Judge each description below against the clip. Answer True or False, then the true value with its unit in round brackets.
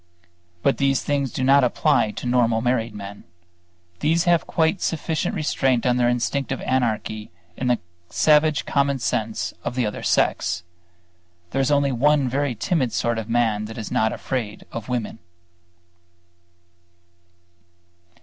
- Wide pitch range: False (3.8 semitones)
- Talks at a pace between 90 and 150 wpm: True (145 wpm)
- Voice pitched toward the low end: True (125 Hz)